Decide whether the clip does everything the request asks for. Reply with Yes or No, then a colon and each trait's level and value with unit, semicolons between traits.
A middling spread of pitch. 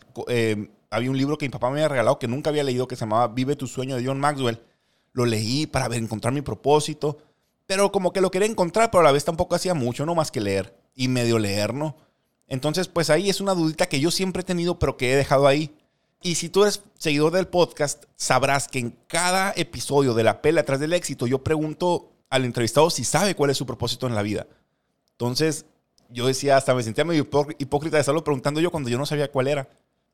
Yes: average, 4.1 semitones